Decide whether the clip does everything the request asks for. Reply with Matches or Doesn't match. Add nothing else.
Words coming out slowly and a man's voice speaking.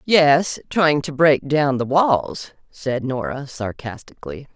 Doesn't match